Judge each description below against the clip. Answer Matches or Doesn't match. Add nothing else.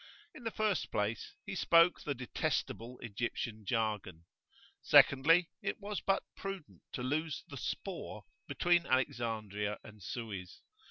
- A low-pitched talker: Matches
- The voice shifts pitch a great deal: Matches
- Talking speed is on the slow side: Matches